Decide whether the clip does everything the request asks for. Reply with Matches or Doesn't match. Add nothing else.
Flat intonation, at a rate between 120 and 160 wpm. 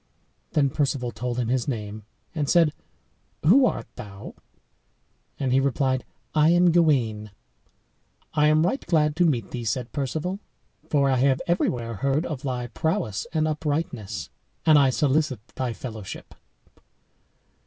Doesn't match